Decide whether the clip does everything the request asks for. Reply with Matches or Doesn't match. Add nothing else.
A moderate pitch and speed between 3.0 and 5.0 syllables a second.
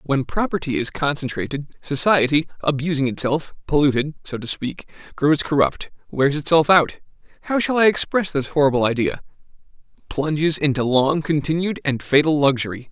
Doesn't match